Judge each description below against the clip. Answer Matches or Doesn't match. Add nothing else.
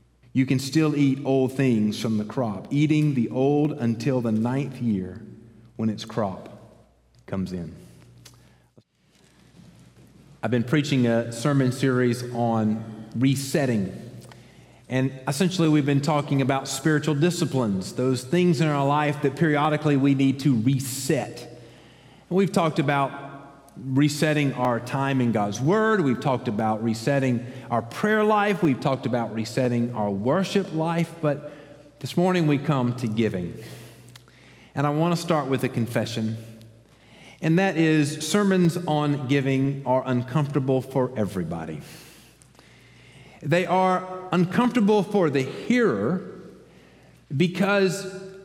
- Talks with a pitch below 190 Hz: Matches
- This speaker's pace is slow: Matches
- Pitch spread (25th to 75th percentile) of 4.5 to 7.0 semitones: Matches